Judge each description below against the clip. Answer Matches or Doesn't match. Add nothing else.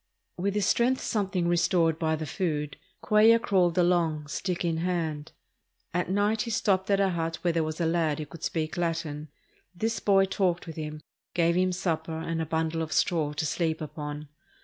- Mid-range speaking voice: Matches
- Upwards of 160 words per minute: Matches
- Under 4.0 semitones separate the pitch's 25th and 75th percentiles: Matches